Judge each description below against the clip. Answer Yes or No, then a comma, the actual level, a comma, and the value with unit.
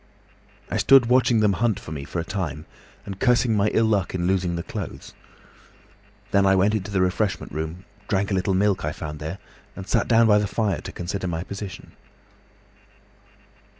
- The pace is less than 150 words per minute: No, average, 185 wpm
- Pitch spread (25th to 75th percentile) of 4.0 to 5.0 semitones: No, average, 3.1 semitones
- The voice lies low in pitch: Yes, very low, 95 Hz